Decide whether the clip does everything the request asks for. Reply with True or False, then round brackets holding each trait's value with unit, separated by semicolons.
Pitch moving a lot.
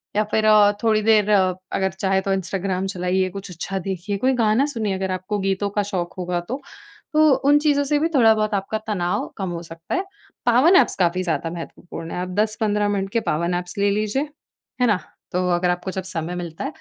False (3.0 semitones)